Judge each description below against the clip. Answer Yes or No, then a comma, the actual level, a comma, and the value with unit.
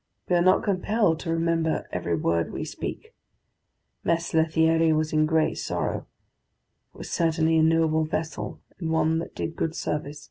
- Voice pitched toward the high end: No, medium, 160 Hz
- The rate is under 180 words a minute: Yes, average, 165 wpm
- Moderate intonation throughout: No, narrow, 0.9 semitones